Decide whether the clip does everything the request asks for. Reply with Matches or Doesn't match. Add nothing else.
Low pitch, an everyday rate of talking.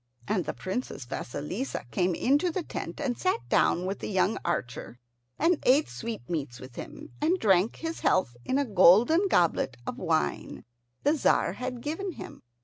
Doesn't match